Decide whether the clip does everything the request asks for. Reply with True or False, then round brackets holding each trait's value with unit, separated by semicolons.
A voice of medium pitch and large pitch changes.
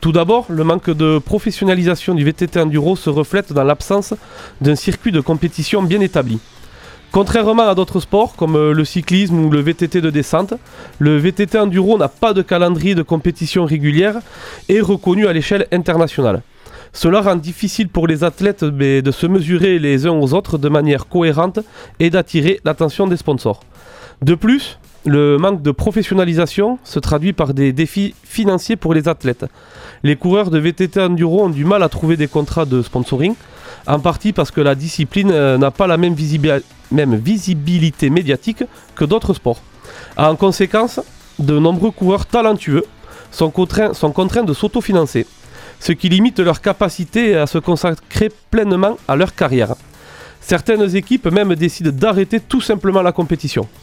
False (175 Hz; 4.5 semitones)